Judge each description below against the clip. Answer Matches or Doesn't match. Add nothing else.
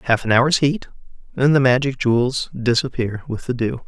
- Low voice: Matches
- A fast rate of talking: Doesn't match